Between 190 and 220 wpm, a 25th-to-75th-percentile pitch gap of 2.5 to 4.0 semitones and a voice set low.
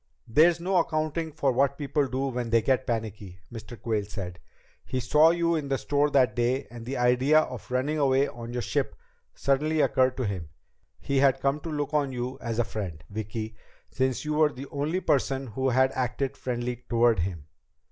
Yes: average, 195 wpm; average, 3.6 semitones; low, 130 Hz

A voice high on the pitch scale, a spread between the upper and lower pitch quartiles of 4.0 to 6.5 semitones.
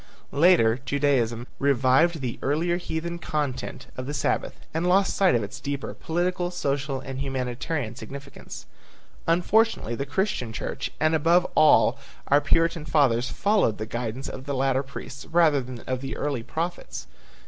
No: medium, 140 Hz; average, 4.4 semitones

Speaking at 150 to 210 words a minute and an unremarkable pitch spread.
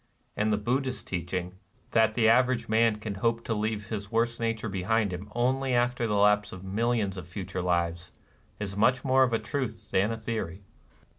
Yes: average, 200 wpm; average, 3.3 semitones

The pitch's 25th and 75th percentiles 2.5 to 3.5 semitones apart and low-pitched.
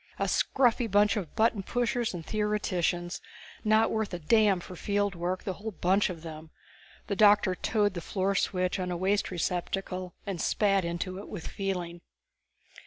No: average, 2.8 semitones; high, 195 Hz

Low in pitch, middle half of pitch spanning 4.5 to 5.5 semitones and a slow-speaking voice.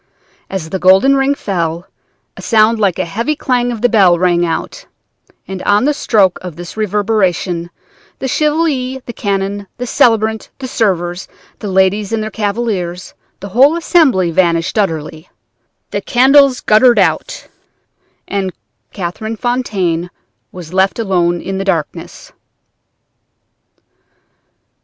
No: high, 200 Hz; average, 5.0 semitones; slow, 130 wpm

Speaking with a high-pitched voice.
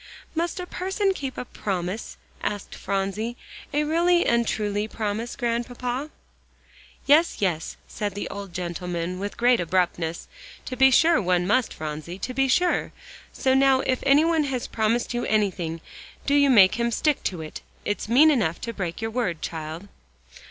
Yes: high, 230 Hz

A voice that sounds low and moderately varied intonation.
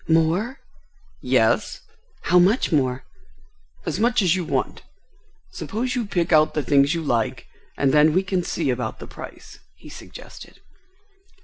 No: medium, 165 Hz; average, 4.9 semitones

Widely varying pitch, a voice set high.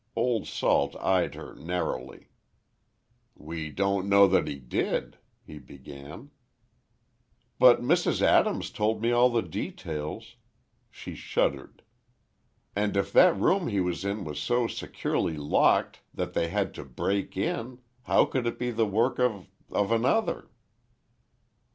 No: wide, 6.3 semitones; low, 100 Hz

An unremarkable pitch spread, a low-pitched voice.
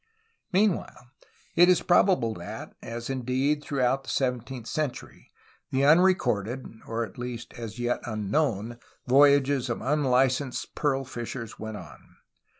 Yes: average, 3.3 semitones; low, 130 Hz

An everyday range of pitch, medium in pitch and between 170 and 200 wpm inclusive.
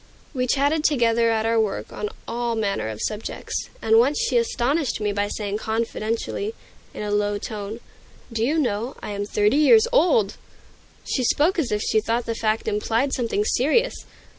No: average, 4.9 semitones; high, 230 Hz; average, 175 wpm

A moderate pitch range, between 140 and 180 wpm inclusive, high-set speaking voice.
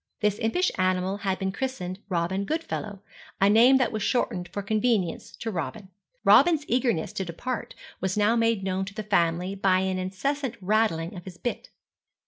Yes: average, 3.7 semitones; average, 170 wpm; high, 200 Hz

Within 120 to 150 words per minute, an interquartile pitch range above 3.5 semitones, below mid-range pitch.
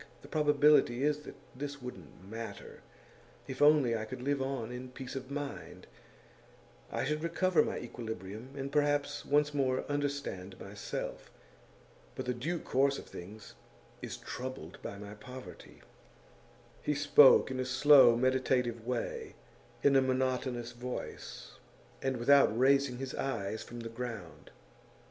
No: average, 140 wpm; average, 3.2 semitones; low, 130 Hz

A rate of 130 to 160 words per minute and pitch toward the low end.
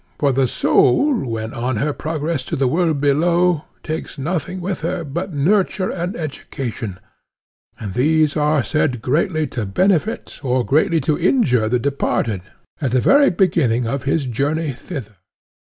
No: average, 150 wpm; medium, 150 Hz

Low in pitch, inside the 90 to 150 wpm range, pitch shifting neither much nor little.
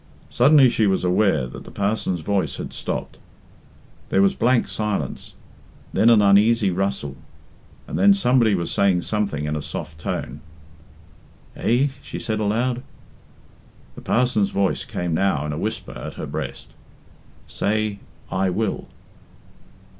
Yes: low, 100 Hz; average, 140 wpm; average, 4.0 semitones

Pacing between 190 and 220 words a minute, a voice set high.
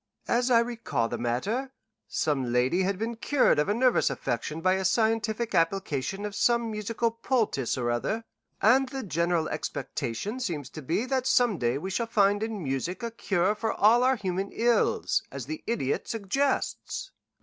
No: average, 170 wpm; high, 205 Hz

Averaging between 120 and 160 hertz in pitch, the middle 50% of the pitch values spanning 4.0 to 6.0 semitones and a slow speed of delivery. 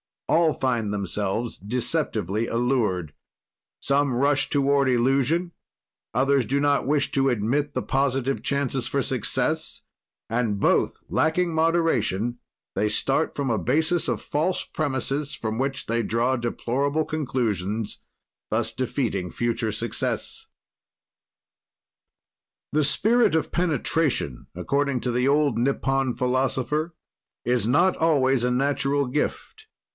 No: low, 135 Hz; average, 3.6 semitones; slow, 115 wpm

